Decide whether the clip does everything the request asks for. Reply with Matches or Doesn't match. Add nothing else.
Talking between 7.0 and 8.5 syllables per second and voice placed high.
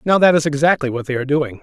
Doesn't match